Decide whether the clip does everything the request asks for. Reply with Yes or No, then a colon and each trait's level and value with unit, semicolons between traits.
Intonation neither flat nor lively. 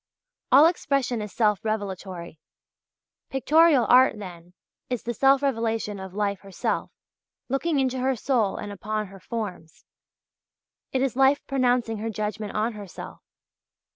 Yes: average, 4.5 semitones